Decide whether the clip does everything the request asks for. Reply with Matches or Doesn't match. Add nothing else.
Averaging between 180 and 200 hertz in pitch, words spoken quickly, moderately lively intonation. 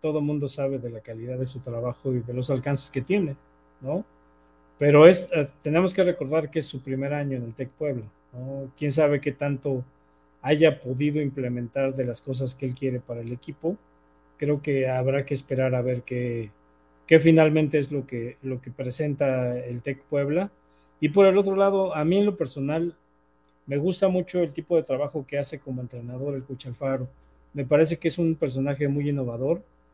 Doesn't match